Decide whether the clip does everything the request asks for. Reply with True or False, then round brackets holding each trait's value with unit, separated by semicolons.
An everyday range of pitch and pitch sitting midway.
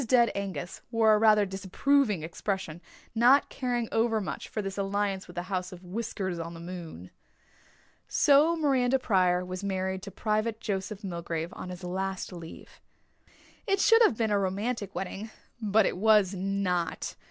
False (3.6 semitones; 195 Hz)